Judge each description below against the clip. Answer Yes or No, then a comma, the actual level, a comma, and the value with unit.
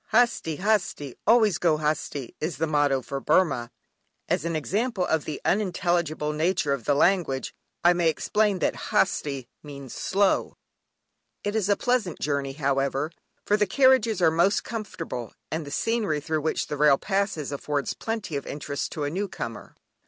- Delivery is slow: No, average, 165 wpm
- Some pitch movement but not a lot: No, wide, 5.8 semitones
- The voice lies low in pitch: No, medium, 160 Hz